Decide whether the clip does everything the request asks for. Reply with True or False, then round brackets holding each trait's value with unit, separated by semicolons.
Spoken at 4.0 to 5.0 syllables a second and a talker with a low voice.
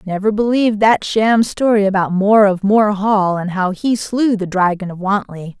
False (4.6 syllables/s; 205 Hz)